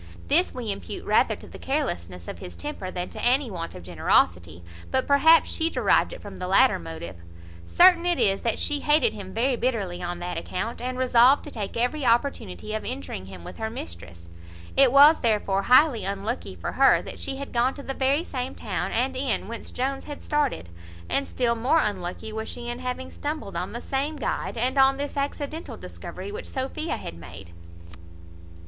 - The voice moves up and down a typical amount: No, wide, 7.0 semitones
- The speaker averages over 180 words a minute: Yes, average, 195 wpm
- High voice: Yes, high, 240 Hz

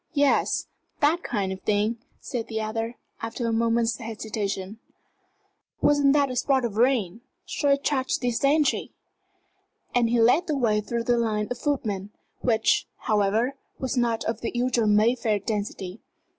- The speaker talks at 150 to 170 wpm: Yes, average, 155 wpm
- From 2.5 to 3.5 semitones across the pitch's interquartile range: Yes, average, 3.1 semitones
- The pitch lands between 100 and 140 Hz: No, high, 230 Hz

